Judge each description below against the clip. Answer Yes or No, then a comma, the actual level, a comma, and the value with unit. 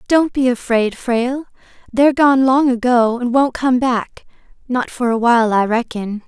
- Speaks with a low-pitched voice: No, high, 245 Hz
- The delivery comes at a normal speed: Yes, average, 165 wpm